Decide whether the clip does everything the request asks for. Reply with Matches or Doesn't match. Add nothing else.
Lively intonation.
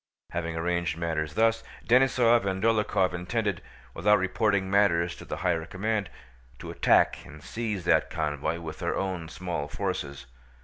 Doesn't match